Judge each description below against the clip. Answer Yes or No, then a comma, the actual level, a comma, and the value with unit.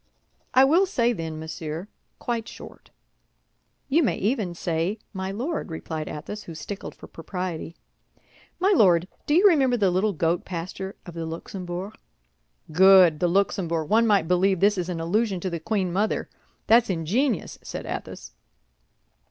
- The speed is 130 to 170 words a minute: Yes, average, 150 wpm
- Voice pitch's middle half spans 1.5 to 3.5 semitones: No, average, 4.6 semitones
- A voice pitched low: No, high, 190 Hz